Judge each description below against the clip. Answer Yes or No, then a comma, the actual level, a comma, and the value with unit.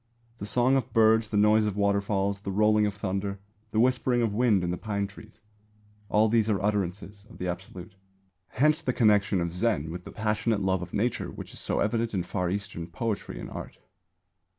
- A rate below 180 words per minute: No, average, 195 wpm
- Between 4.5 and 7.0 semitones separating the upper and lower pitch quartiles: No, narrow, 2.4 semitones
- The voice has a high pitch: No, low, 105 Hz